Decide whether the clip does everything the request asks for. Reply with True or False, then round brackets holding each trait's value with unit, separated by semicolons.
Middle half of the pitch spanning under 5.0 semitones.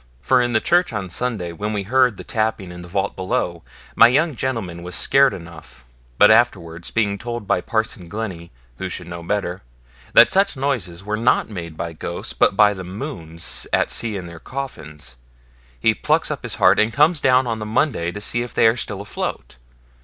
False (5.4 semitones)